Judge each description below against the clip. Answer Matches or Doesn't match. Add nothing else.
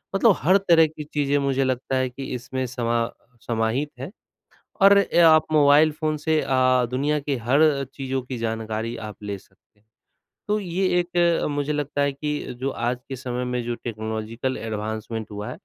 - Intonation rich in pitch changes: Doesn't match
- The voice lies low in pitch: Matches